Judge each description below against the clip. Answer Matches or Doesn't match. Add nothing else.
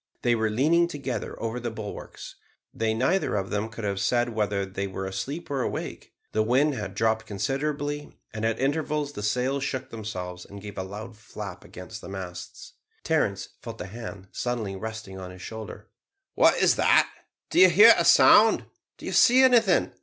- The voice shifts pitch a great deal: Matches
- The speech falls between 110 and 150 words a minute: Doesn't match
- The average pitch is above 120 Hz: Doesn't match